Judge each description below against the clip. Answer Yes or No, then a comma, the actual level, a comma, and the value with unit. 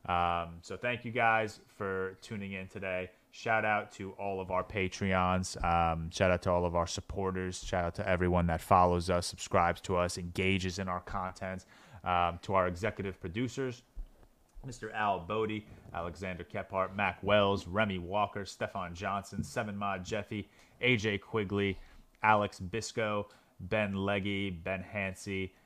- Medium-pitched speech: No, very low, 95 Hz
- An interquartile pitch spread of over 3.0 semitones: No, narrow, 2.4 semitones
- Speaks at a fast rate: No, average, 150 wpm